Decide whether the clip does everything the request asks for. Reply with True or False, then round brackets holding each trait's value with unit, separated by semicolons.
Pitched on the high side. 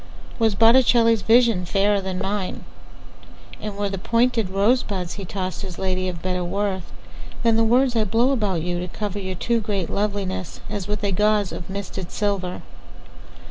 True (200 Hz)